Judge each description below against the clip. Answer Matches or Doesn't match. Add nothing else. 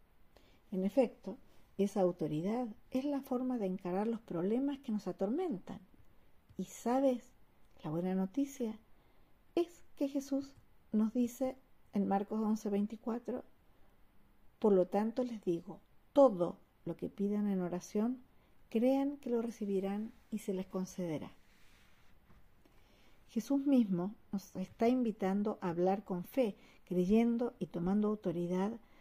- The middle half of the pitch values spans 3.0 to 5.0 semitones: Matches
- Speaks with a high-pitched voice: Matches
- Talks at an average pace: Doesn't match